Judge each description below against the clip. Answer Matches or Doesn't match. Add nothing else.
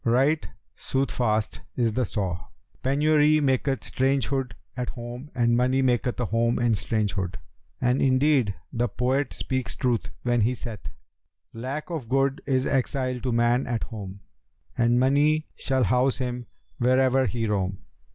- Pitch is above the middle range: Doesn't match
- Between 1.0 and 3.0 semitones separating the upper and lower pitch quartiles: Matches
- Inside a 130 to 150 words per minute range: Matches